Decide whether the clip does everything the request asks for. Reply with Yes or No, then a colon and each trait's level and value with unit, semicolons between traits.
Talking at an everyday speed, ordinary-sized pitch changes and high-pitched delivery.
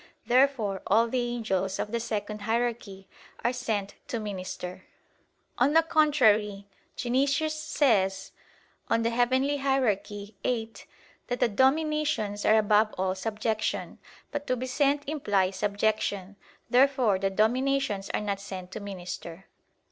No: slow, 125 wpm; average, 4.4 semitones; high, 220 Hz